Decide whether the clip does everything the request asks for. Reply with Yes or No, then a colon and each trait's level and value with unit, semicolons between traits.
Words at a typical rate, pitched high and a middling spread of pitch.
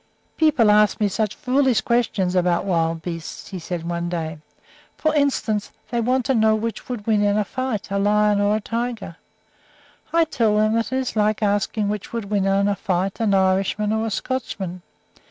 Yes: average, 190 wpm; high, 210 Hz; average, 3.0 semitones